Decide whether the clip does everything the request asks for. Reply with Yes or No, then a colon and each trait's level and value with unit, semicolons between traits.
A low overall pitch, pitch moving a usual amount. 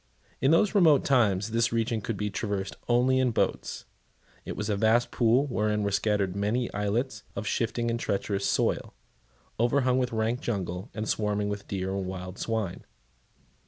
Yes: low, 110 Hz; average, 3.1 semitones